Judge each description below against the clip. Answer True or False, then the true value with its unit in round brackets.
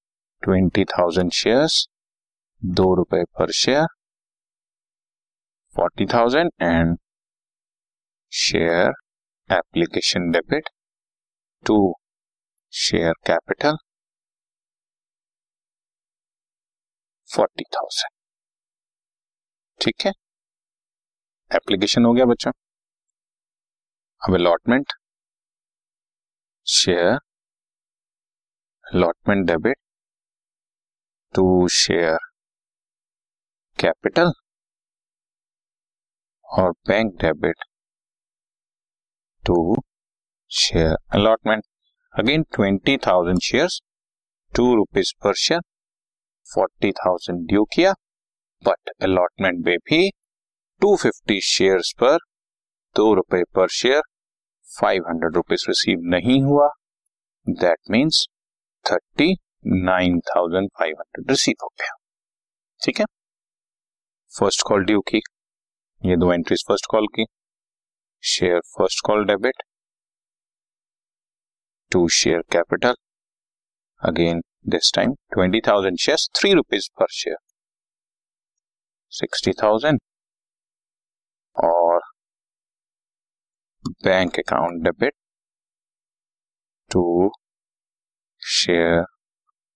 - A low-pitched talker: True (95 Hz)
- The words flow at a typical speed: False (70 wpm)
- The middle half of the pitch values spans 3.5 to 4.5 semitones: False (5.0 semitones)